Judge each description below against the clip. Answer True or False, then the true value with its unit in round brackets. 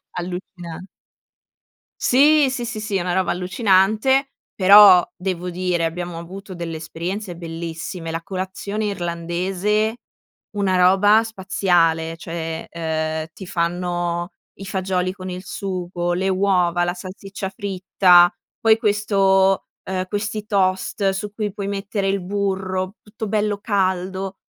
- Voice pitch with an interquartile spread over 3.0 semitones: False (2.4 semitones)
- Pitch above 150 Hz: True (185 Hz)